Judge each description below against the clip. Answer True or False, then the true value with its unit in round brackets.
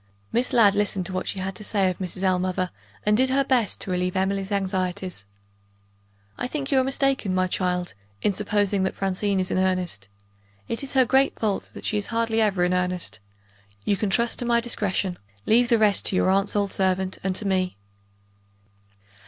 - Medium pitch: False (195 Hz)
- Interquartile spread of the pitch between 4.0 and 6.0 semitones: False (3.2 semitones)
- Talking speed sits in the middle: True (195 wpm)